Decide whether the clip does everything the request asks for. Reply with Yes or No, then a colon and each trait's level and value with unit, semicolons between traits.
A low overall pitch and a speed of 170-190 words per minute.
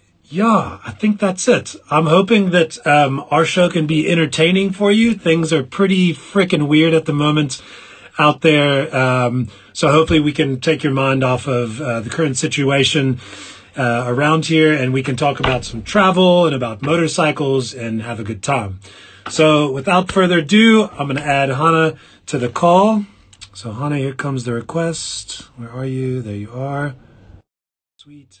No: medium, 145 Hz; average, 175 wpm